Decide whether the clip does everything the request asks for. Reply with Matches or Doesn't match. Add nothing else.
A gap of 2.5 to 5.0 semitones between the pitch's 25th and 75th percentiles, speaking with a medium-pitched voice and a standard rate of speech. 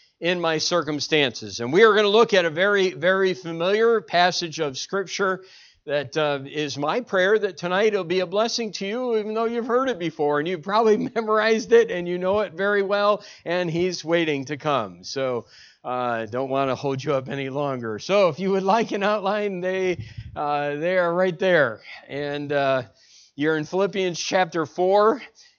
Doesn't match